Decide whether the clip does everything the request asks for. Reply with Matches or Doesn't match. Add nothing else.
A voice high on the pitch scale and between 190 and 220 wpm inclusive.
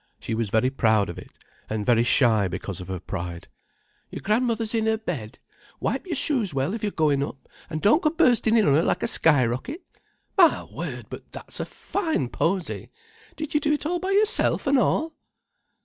Doesn't match